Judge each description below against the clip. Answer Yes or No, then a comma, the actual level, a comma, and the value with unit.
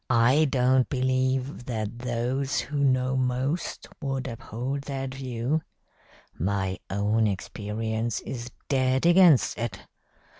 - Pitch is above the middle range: No, low, 130 Hz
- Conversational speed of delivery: No, slow, 110 wpm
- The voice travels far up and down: No, narrow, 2.6 semitones